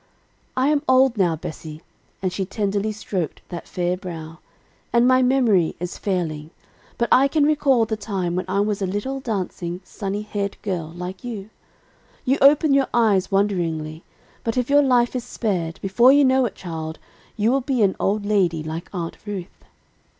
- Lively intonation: Yes, wide, 5.7 semitones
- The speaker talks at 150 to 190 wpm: Yes, average, 175 wpm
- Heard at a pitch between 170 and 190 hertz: No, high, 200 Hz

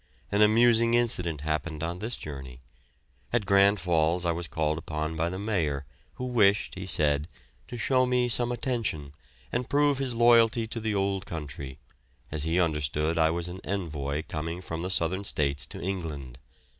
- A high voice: No, very low, 90 Hz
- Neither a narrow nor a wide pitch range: No, wide, 6.3 semitones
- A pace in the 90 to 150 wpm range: No, average, 170 wpm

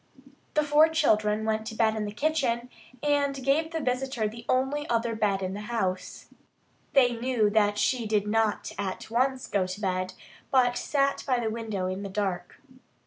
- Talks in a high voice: Yes, high, 230 Hz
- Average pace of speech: Yes, average, 180 wpm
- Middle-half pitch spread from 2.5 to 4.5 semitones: Yes, average, 4.2 semitones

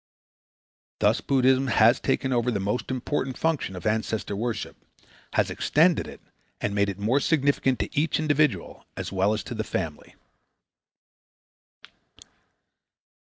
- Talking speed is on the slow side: Yes, slow, 130 wpm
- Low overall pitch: Yes, low, 125 Hz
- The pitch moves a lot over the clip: No, average, 4.8 semitones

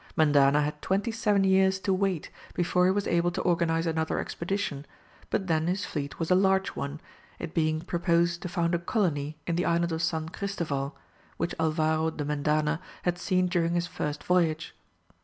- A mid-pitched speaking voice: Yes, medium, 170 Hz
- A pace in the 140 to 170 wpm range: No, average, 180 wpm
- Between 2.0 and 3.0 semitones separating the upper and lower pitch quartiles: Yes, narrow, 2.6 semitones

